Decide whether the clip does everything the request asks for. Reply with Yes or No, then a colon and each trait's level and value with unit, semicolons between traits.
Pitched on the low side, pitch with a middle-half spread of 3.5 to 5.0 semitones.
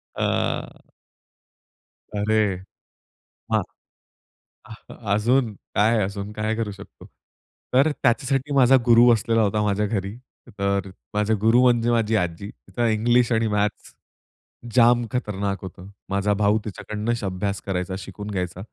No: low, 105 Hz; average, 2.8 semitones